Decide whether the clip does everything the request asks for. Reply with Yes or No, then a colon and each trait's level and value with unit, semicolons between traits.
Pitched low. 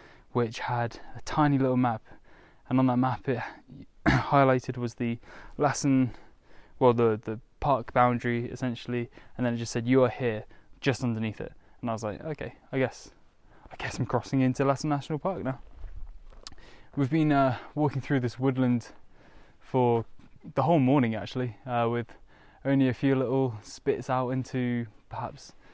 Yes: low, 125 Hz